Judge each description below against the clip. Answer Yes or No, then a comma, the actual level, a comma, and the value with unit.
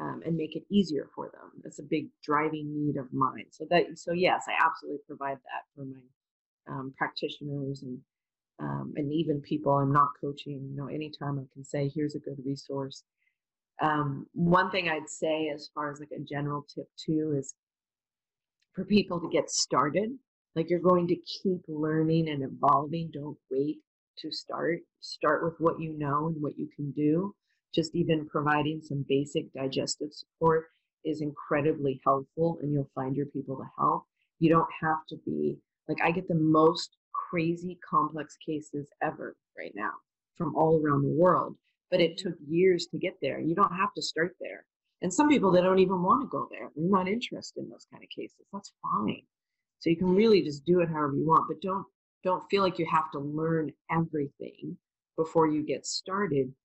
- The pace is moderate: Yes, average, 190 wpm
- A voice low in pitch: No, medium, 155 Hz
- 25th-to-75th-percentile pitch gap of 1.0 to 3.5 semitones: Yes, average, 3.0 semitones